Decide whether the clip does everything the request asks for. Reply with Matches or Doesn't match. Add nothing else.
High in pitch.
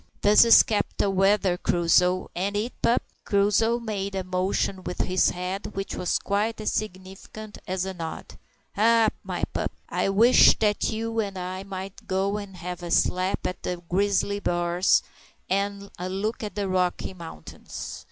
Matches